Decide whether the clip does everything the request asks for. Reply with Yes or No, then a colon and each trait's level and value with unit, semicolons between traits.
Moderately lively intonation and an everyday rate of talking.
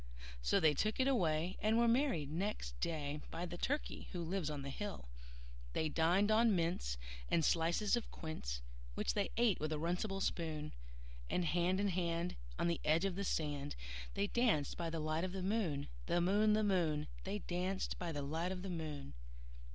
Yes: average, 4.1 semitones; average, 190 wpm